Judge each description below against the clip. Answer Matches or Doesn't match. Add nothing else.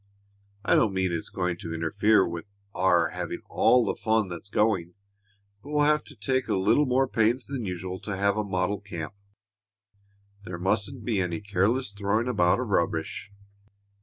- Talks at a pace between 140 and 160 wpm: Doesn't match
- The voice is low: Matches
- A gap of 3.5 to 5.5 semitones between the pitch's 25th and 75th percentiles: Matches